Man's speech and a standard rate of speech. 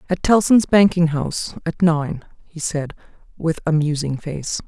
No: female; average, 155 wpm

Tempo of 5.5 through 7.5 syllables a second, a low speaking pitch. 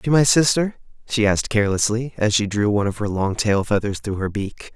Yes: 5.7 syllables/s; low, 110 Hz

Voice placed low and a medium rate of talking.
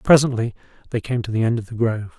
No: low, 115 Hz; fast, 245 wpm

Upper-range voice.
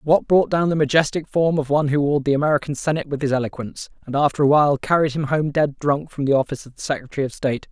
No: medium, 145 Hz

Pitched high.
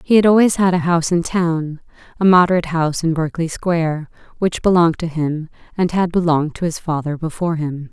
No: medium, 165 Hz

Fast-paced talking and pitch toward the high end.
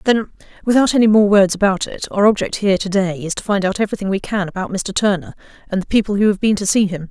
Yes: fast, 260 wpm; high, 200 Hz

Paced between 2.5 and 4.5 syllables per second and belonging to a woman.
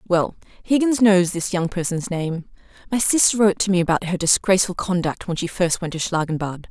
No: 5.7 syllables/s; female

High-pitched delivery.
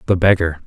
No: very low, 85 Hz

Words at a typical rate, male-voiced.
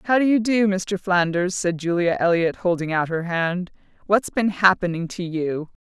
No: average, 175 wpm; female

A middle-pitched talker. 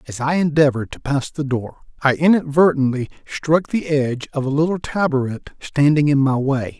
Yes: medium, 145 Hz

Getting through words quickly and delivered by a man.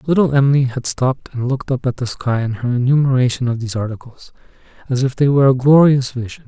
Yes: fast, 215 wpm; male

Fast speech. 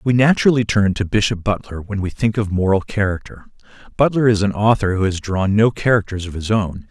Yes: fast, 210 wpm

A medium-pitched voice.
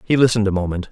No: low, 105 Hz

